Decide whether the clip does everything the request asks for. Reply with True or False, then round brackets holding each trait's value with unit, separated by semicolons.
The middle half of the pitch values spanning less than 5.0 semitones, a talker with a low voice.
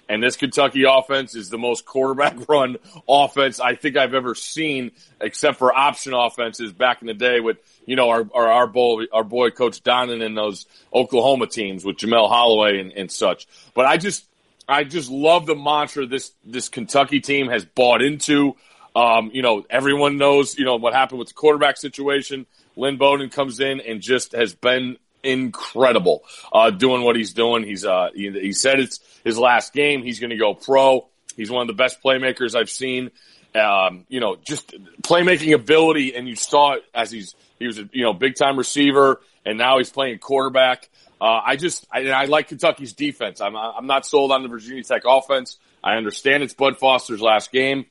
True (2.8 semitones; 130 Hz)